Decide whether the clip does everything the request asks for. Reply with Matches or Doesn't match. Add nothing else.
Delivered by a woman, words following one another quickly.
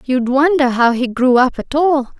Matches